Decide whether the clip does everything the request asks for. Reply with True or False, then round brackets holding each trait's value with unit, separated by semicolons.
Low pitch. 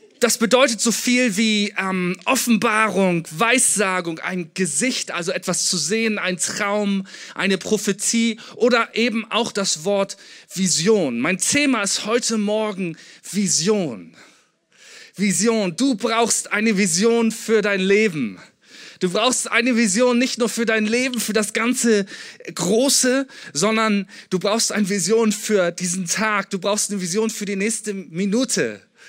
False (215 Hz)